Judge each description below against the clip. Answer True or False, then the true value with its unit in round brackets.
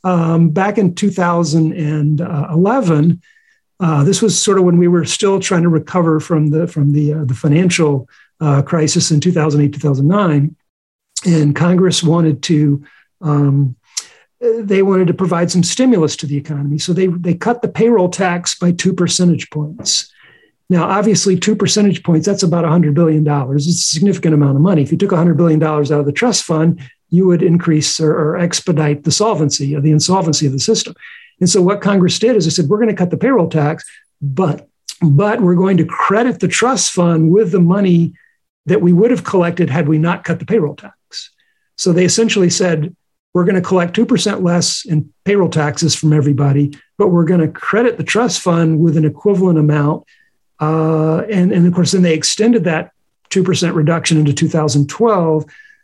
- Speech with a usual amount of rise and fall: True (3.8 semitones)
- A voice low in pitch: False (170 Hz)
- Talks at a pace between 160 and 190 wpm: True (185 wpm)